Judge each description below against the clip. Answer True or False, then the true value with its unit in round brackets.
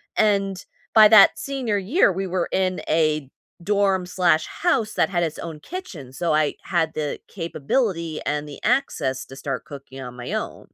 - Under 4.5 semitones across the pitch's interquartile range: False (5.2 semitones)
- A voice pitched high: False (175 Hz)